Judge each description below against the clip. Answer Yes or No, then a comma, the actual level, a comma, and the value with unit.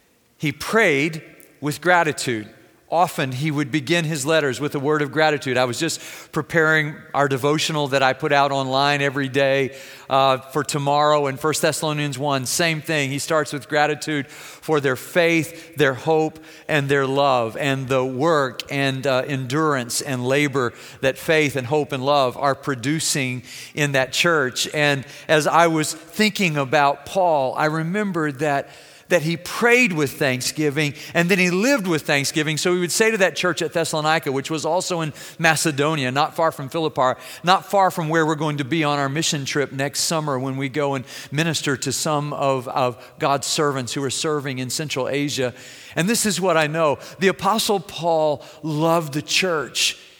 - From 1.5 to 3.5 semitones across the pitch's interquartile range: Yes, average, 2.8 semitones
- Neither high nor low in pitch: Yes, medium, 150 Hz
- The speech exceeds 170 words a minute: Yes, average, 180 wpm